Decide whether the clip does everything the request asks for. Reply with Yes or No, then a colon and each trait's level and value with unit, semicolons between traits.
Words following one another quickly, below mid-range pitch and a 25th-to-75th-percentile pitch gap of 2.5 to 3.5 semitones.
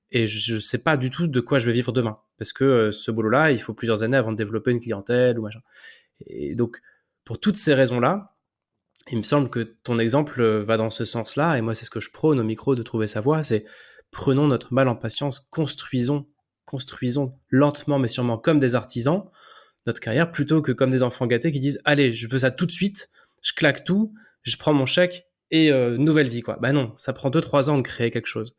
No: fast, 235 wpm; low, 130 Hz; average, 4.1 semitones